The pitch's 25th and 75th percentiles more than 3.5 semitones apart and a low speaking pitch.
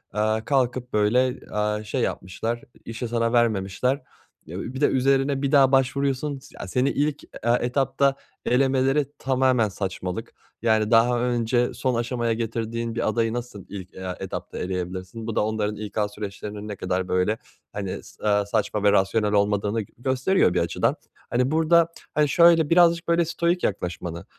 Yes: average, 4.3 semitones; low, 115 Hz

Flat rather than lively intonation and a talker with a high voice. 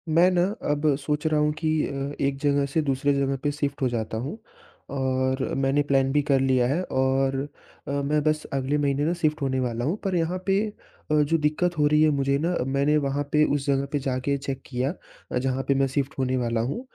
No: narrow, 2.1 semitones; medium, 140 Hz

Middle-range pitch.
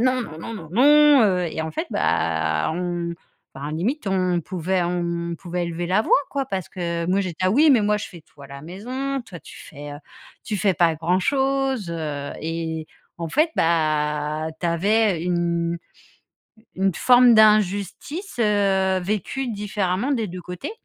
Yes: medium, 180 Hz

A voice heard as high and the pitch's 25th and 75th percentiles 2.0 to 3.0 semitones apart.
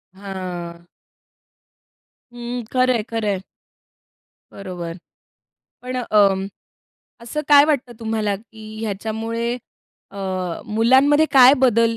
No: high, 225 Hz; average, 3.7 semitones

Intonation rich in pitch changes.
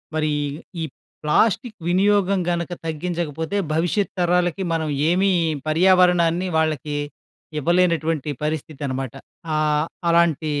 No: average, 2.7 semitones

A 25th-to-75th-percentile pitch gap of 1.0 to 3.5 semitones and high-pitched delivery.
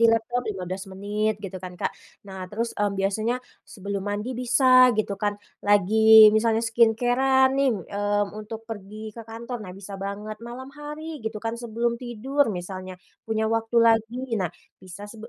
Yes: average, 2.7 semitones; high, 220 Hz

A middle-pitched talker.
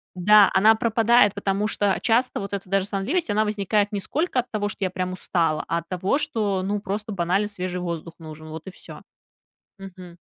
No: high, 200 Hz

